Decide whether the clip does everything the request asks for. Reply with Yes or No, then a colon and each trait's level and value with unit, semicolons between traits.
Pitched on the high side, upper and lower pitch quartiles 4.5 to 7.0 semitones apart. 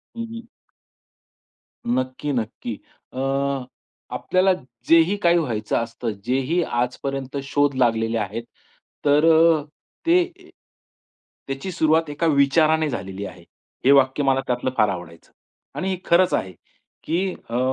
No: medium, 140 Hz; average, 5.2 semitones